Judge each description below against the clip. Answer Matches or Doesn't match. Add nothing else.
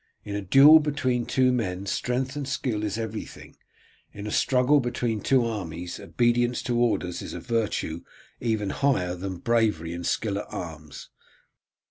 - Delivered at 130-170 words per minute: Matches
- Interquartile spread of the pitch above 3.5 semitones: Matches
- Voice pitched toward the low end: Matches